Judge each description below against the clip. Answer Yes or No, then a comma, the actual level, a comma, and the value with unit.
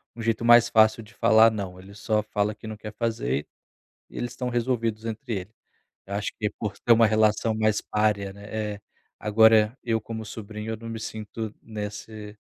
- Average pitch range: No, narrow, 1.4 semitones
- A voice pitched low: Yes, low, 110 Hz